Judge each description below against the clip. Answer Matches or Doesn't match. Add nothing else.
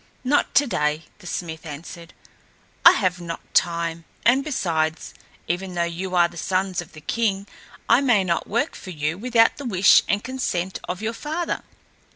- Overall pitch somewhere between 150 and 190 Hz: Matches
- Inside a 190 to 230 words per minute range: Doesn't match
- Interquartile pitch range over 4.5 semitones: Matches